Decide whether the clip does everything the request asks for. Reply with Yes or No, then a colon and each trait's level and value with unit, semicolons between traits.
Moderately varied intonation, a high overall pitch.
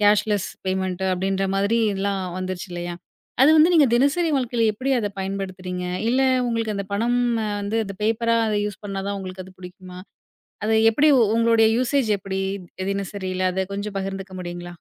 Yes: average, 3.4 semitones; high, 200 Hz